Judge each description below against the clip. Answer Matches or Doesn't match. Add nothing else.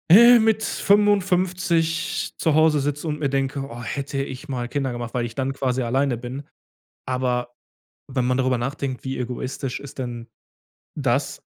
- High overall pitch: Doesn't match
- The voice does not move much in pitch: Doesn't match